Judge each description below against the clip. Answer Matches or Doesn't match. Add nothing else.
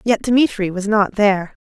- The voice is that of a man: Doesn't match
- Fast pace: Doesn't match